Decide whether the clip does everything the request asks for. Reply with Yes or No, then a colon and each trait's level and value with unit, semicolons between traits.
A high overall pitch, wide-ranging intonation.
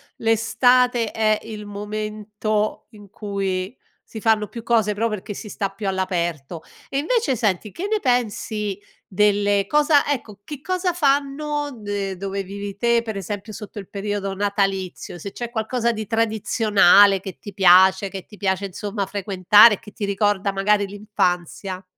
No: high, 205 Hz; narrow, 2.5 semitones